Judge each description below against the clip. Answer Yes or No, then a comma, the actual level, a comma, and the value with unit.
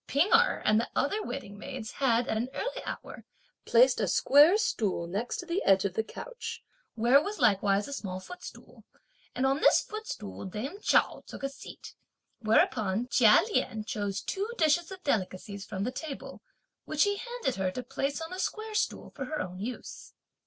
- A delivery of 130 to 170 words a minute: No, average, 185 wpm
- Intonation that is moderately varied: No, wide, 7.5 semitones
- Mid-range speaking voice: No, very high, 255 Hz